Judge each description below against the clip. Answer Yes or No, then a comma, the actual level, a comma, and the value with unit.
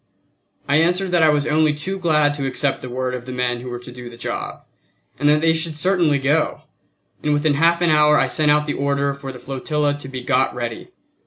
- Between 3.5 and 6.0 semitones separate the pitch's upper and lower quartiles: No, average, 3.1 semitones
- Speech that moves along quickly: Yes, fast, 235 wpm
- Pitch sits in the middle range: Yes, medium, 145 Hz